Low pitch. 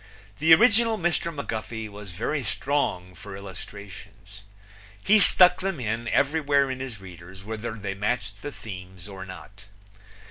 Yes: low, 110 Hz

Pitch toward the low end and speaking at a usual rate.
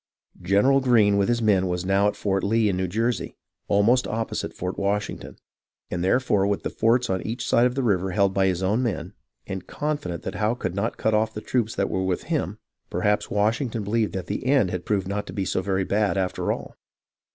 No: low, 100 Hz; fast, 220 wpm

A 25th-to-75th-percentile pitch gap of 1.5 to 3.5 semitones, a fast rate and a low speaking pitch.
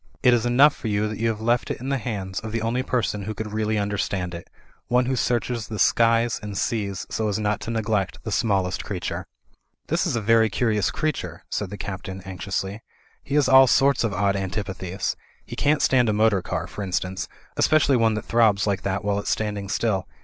Yes: average, 2.9 semitones; fast, 215 wpm; low, 110 Hz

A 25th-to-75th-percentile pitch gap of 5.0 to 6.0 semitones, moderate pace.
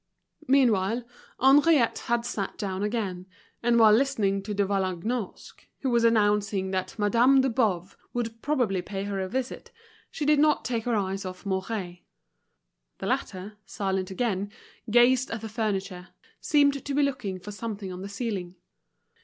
No: average, 4.0 semitones; average, 155 wpm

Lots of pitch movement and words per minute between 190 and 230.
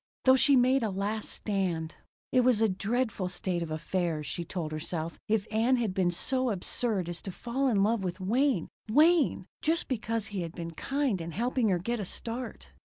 Yes: wide, 5.8 semitones; average, 195 wpm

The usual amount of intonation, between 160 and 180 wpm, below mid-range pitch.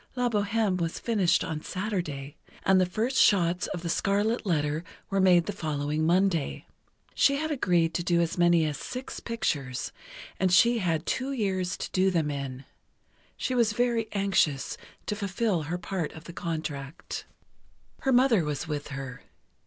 No: average, 4.9 semitones; average, 165 wpm; medium, 180 Hz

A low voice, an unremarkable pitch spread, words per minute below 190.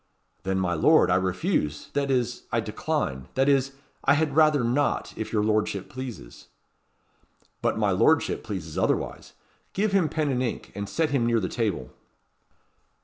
No: low, 120 Hz; wide, 6.8 semitones; average, 160 wpm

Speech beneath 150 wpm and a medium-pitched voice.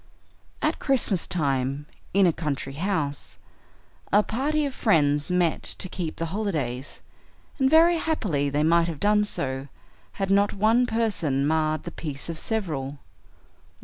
Yes: average, 140 wpm; medium, 170 Hz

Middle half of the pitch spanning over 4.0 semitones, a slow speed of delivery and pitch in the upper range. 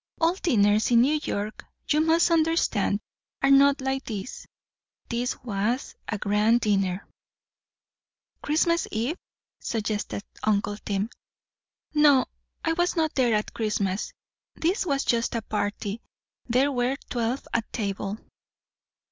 Yes: wide, 5.6 semitones; slow, 120 wpm; high, 235 Hz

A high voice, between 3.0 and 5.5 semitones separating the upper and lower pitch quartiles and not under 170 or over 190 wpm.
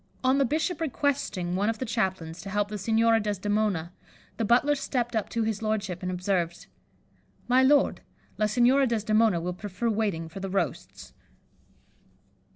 No: high, 215 Hz; average, 4.0 semitones; average, 160 wpm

